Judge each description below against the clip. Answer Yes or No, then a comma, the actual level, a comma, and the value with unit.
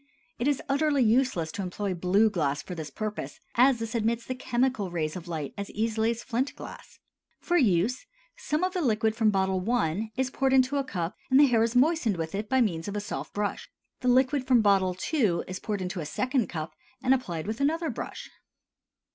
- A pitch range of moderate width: No, wide, 5.7 semitones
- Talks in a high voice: Yes, high, 220 Hz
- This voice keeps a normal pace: No, fast, 210 wpm